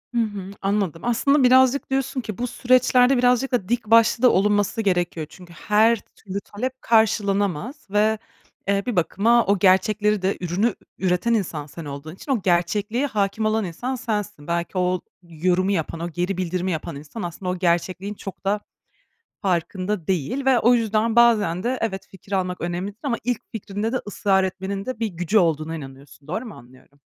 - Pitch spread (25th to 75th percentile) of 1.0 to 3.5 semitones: No, average, 4.3 semitones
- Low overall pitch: No, high, 200 Hz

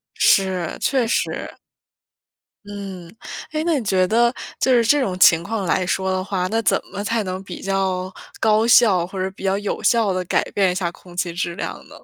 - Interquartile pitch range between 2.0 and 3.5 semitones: Yes, average, 3.2 semitones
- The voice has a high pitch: Yes, high, 195 Hz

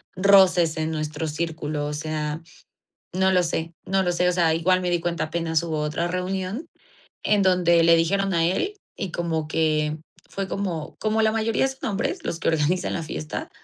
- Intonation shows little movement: No, average, 3.0 semitones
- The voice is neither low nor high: Yes, medium, 170 Hz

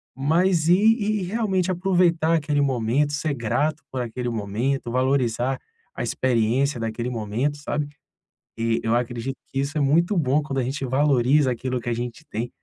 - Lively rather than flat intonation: No, average, 3.8 semitones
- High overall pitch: No, low, 135 Hz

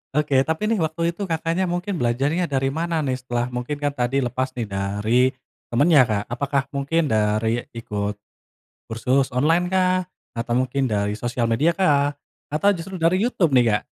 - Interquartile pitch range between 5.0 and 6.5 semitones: Yes, wide, 5.6 semitones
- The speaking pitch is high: No, medium, 140 Hz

